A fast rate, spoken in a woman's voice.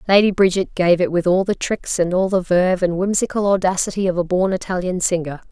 Yes: fast, 220 wpm; female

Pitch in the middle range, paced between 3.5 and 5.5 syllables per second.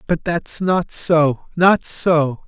No: medium, 165 Hz; 2.7 syllables/s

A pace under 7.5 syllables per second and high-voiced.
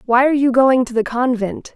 Yes: 5.6 syllables/s; very high, 250 Hz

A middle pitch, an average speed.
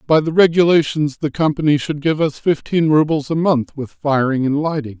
Yes: medium, 150 Hz; average, 190 wpm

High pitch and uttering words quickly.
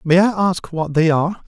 No: medium, 170 Hz; fast, 245 wpm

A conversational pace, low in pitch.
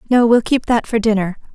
No: average, 195 wpm; high, 225 Hz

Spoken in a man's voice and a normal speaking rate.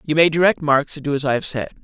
No: male; fast, 330 wpm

